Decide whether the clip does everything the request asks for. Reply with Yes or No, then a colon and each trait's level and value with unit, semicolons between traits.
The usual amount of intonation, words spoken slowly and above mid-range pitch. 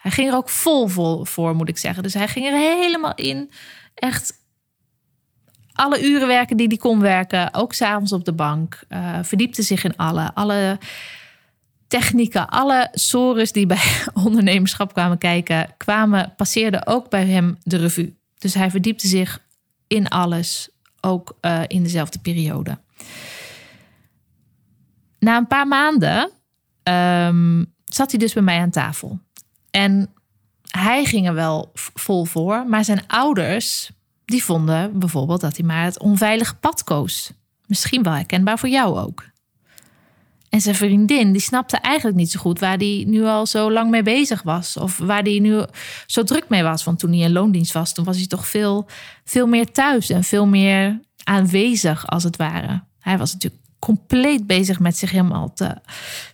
No: average, 4.2 semitones; average, 165 wpm; high, 195 Hz